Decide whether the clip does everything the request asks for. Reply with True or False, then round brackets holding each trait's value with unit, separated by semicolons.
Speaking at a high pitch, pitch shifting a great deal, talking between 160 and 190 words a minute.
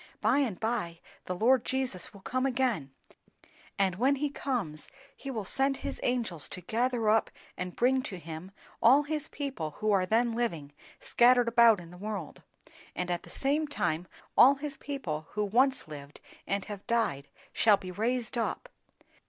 True (225 Hz; 6.1 semitones; 170 wpm)